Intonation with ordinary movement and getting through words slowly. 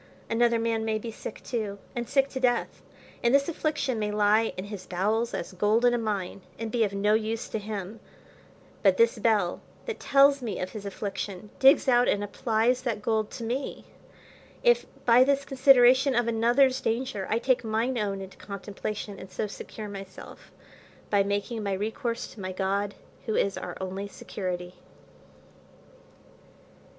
No: average, 3.3 semitones; average, 170 wpm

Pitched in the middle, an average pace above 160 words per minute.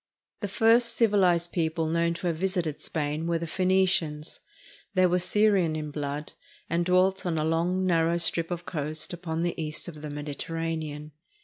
Yes: medium, 170 Hz; average, 170 wpm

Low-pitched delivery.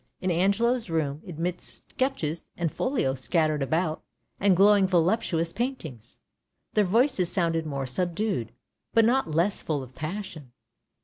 No: medium, 170 Hz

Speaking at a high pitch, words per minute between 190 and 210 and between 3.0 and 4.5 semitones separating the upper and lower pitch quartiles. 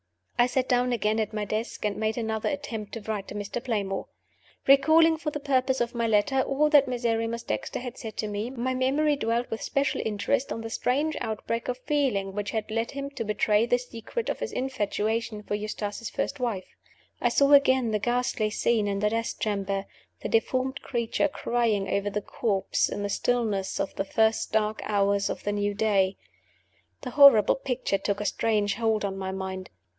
Yes: high, 225 Hz; average, 195 wpm; average, 3.6 semitones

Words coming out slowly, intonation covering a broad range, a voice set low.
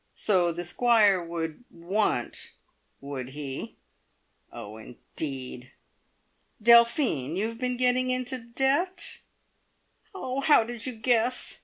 No: slow, 110 wpm; wide, 7.7 semitones; high, 220 Hz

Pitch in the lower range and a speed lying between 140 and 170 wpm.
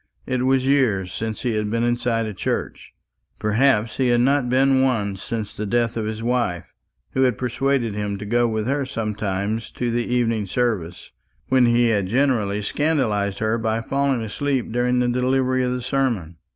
No: low, 120 Hz; average, 180 wpm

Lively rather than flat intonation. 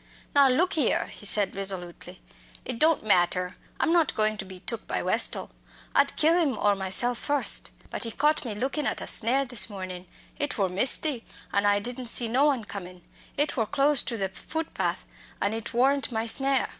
Yes: wide, 5.7 semitones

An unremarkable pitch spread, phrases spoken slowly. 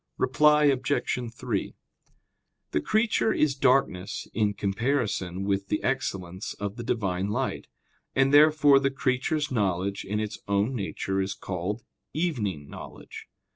No: wide, 5.8 semitones; slow, 130 wpm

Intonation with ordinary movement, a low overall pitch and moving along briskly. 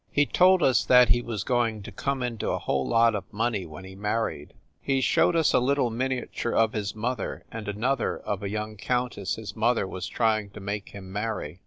Yes: average, 3.4 semitones; low, 110 Hz; fast, 215 wpm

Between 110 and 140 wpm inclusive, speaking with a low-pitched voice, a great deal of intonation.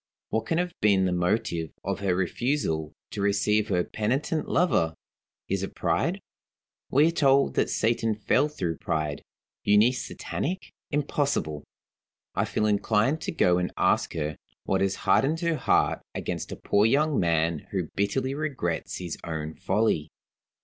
No: average, 150 wpm; low, 105 Hz; wide, 7.8 semitones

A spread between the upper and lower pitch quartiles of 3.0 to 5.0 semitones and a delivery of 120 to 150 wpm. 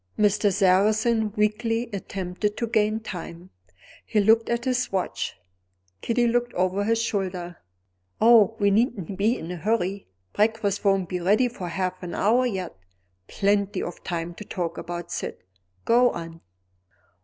Yes: average, 3.6 semitones; average, 145 wpm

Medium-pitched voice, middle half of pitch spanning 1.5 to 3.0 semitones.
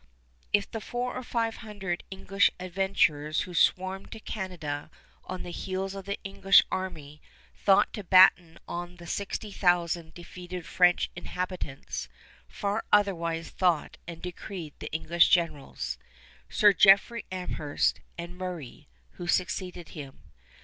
Yes: medium, 180 Hz; narrow, 2.6 semitones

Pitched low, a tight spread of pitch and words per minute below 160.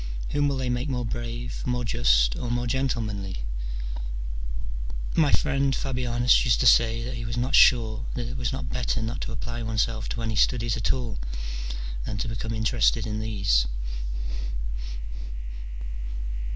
Yes: low, 120 Hz; narrow, 2.0 semitones; average, 150 wpm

